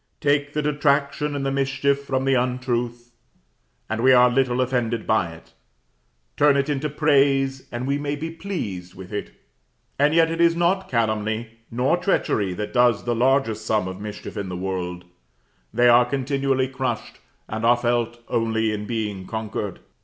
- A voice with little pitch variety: No, average, 4.2 semitones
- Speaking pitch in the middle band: No, low, 125 Hz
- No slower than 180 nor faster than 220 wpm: No, average, 170 wpm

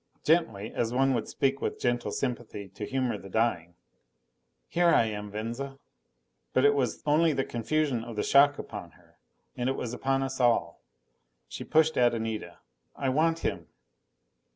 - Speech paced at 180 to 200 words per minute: No, average, 165 wpm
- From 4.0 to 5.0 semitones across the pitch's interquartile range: No, average, 3.6 semitones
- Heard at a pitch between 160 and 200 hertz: No, low, 125 Hz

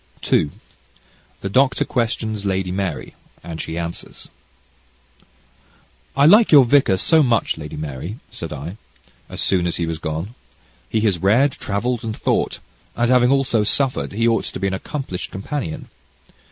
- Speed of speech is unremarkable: Yes, average, 155 wpm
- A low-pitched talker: Yes, low, 105 Hz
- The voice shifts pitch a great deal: Yes, wide, 6.3 semitones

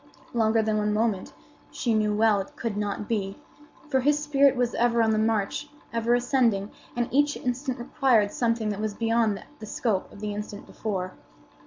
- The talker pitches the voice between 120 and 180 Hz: No, high, 225 Hz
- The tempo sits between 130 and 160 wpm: No, average, 180 wpm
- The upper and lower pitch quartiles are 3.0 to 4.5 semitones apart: No, narrow, 2.6 semitones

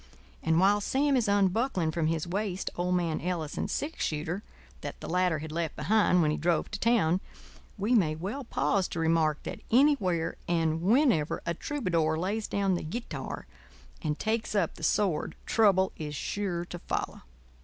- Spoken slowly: No, average, 170 wpm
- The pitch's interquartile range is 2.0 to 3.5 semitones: No, average, 4.4 semitones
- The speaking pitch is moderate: Yes, medium, 180 Hz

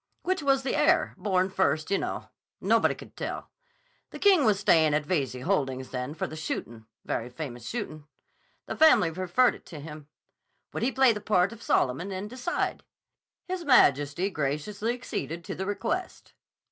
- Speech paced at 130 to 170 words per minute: Yes, average, 165 wpm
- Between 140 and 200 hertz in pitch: Yes, medium, 185 Hz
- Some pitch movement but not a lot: No, wide, 8.3 semitones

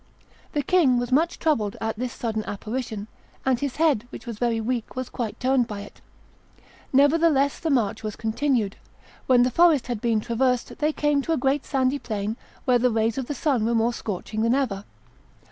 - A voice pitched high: Yes, high, 245 Hz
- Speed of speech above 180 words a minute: Yes, average, 195 wpm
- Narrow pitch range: No, average, 3.8 semitones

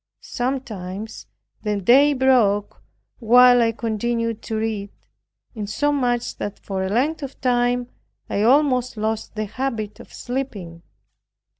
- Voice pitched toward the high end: Yes, high, 230 Hz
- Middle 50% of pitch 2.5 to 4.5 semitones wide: Yes, average, 3.1 semitones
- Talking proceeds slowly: Yes, slow, 120 wpm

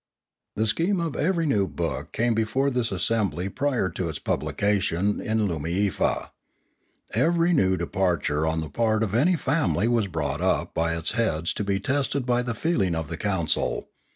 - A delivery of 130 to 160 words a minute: No, average, 170 wpm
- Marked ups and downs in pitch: Yes, wide, 6.6 semitones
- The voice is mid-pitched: No, low, 105 Hz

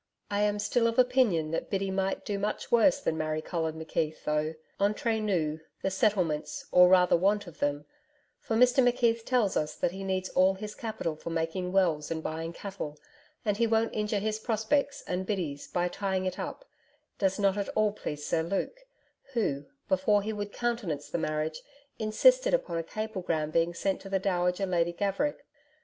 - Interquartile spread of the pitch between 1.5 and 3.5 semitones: No, average, 4.5 semitones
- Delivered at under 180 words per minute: No, average, 185 wpm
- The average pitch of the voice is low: No, high, 195 Hz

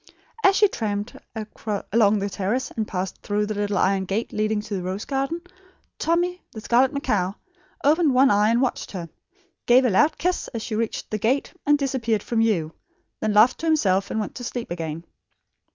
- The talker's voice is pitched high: Yes, high, 220 Hz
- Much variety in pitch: No, average, 4.6 semitones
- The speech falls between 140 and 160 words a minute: No, average, 190 wpm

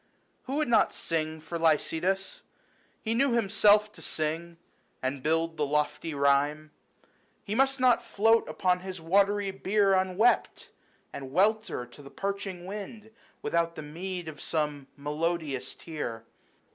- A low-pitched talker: No, medium, 170 Hz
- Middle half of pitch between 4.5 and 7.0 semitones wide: Yes, average, 5.1 semitones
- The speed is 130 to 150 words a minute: Yes, average, 140 wpm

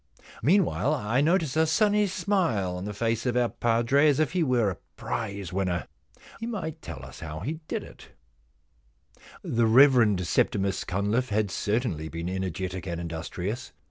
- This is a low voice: Yes, low, 115 Hz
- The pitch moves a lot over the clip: Yes, wide, 7.7 semitones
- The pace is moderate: Yes, average, 160 wpm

